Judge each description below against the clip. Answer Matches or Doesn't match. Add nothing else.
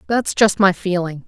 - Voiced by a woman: Matches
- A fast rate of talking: Doesn't match